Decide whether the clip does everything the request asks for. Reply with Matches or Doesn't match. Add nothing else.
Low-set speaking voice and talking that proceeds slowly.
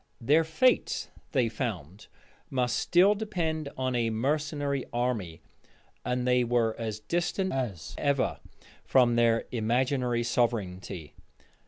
Matches